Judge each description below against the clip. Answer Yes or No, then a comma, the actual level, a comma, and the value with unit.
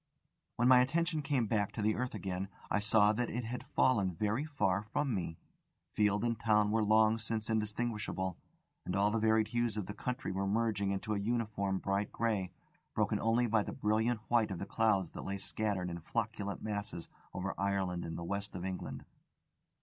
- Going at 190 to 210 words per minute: Yes, average, 195 wpm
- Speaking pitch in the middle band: No, low, 105 Hz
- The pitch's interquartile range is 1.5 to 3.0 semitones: Yes, narrow, 2.6 semitones